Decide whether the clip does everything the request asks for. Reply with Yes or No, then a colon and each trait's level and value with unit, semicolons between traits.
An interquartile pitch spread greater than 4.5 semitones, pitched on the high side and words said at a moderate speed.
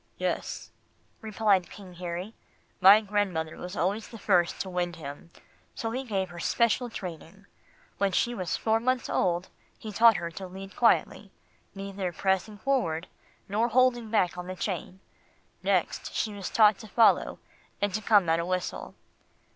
No: average, 3.5 semitones; high, 195 Hz; average, 160 wpm